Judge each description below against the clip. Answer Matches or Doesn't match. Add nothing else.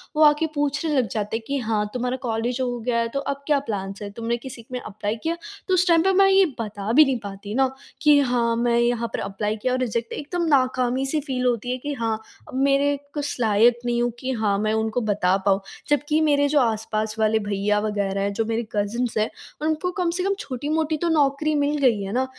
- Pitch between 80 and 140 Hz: Doesn't match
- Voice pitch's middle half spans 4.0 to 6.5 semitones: Matches